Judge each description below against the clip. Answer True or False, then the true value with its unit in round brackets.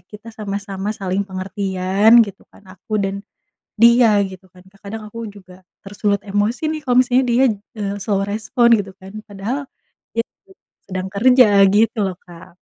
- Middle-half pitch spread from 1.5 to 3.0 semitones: True (2.7 semitones)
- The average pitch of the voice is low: False (205 Hz)